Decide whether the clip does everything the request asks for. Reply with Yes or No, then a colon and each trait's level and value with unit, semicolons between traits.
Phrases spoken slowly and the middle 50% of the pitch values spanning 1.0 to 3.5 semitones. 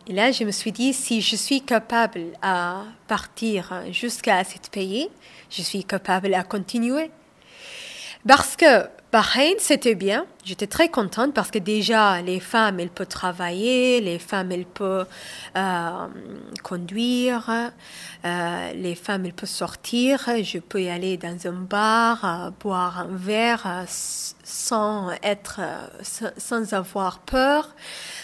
No: slow, 140 wpm; average, 4.1 semitones